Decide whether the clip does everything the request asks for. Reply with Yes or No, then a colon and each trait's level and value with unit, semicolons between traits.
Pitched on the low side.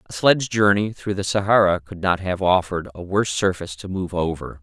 Yes: very low, 95 Hz